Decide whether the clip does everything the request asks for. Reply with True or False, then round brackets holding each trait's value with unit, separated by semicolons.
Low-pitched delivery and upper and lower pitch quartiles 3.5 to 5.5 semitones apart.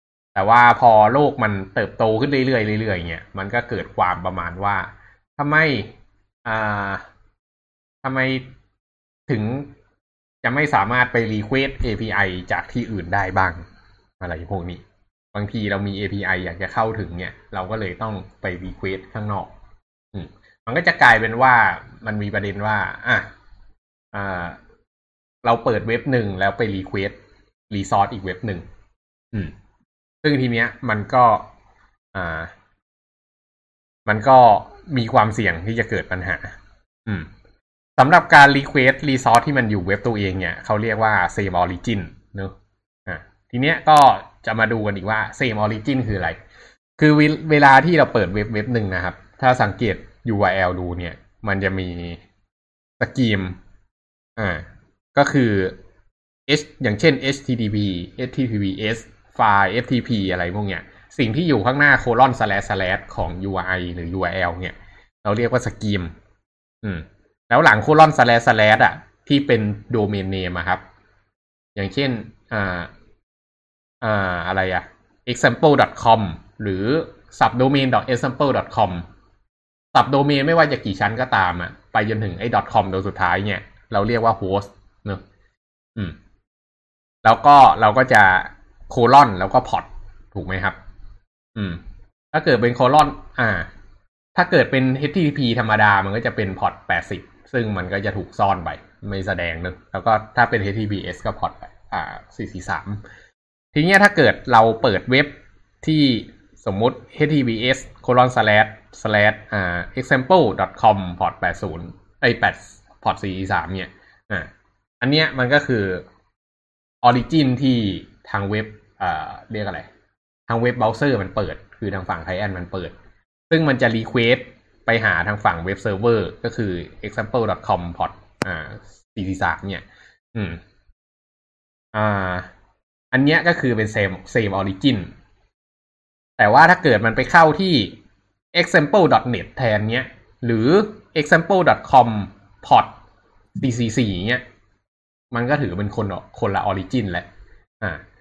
True (105 Hz; 4.2 semitones)